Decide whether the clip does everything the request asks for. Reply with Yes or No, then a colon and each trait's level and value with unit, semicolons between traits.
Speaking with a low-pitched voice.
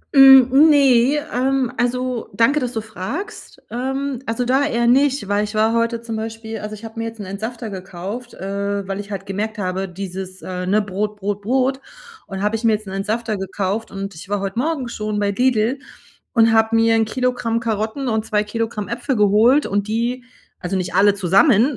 No: high, 220 Hz